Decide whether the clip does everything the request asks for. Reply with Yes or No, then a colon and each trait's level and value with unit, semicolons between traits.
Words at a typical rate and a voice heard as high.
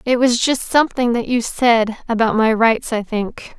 Yes: average, 185 wpm; high, 235 Hz